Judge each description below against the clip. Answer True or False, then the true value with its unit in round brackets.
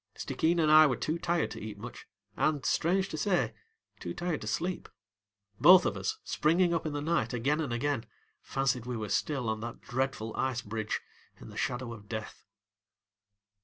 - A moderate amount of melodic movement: False (5.7 semitones)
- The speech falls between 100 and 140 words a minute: False (185 wpm)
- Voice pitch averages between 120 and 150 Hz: True (135 Hz)